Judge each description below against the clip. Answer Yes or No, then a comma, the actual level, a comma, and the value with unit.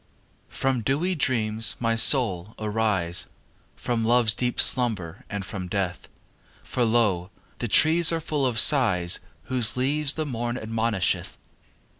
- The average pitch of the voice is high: No, low, 115 Hz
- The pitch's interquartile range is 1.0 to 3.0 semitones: No, average, 3.9 semitones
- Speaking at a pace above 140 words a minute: No, slow, 135 wpm